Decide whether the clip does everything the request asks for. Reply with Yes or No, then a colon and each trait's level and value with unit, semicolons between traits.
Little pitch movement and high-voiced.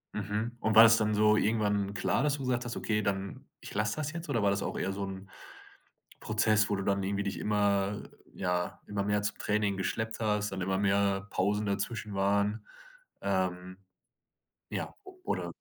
No: narrow, 1.5 semitones; low, 105 Hz